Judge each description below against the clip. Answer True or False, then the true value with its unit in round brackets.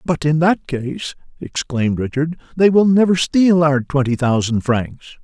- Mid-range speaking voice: True (150 Hz)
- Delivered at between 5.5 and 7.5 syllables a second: False (4.4 syllables/s)